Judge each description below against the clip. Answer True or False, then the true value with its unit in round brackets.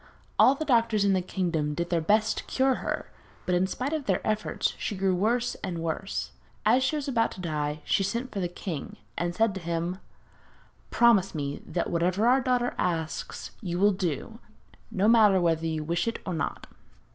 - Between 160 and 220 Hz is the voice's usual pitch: True (190 Hz)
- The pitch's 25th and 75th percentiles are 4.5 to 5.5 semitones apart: True (5.1 semitones)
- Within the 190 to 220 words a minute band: True (195 wpm)